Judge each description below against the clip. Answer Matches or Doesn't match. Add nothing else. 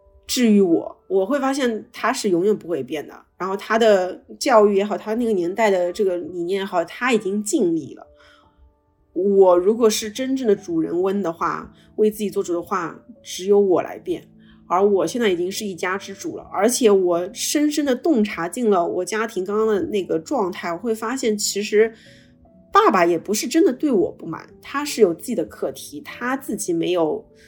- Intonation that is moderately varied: Matches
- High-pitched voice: Matches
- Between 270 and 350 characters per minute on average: Matches